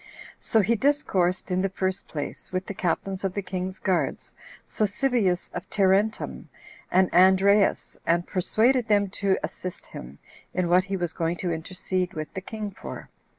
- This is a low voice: No, high, 190 Hz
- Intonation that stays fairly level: Yes, narrow, 2.0 semitones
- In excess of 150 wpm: Yes, average, 160 wpm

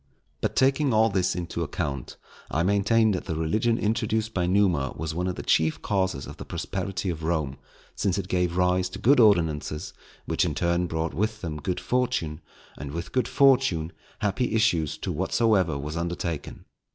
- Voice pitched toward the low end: Yes, very low, 90 Hz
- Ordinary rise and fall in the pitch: Yes, average, 5.0 semitones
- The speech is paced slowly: No, average, 175 wpm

